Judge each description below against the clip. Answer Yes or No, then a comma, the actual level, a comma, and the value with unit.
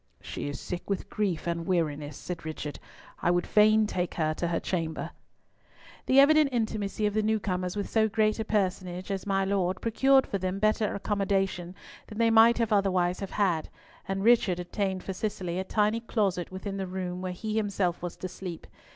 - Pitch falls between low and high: No, high, 195 Hz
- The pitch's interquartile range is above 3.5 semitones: No, average, 3.2 semitones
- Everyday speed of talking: Yes, average, 190 wpm